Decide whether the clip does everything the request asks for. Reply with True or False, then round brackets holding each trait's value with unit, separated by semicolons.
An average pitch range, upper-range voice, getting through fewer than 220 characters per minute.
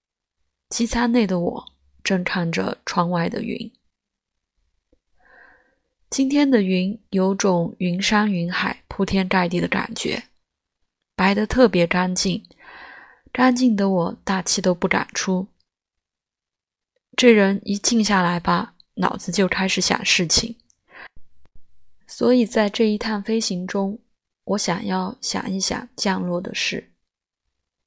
True (3.7 semitones; 195 Hz; 170 characters per minute)